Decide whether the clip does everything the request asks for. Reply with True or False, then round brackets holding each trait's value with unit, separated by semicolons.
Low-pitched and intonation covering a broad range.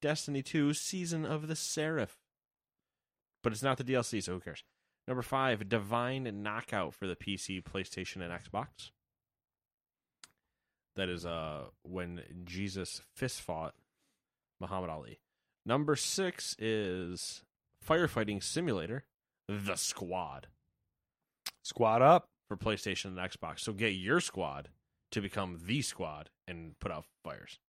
True (100 Hz; 6.5 semitones)